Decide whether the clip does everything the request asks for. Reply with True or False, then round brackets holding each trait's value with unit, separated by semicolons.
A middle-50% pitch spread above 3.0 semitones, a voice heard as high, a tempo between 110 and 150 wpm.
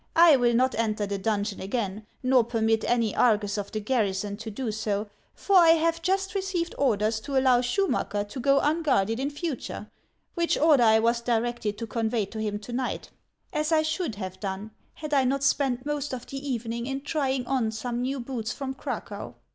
False (4.3 semitones; 245 Hz; 195 wpm)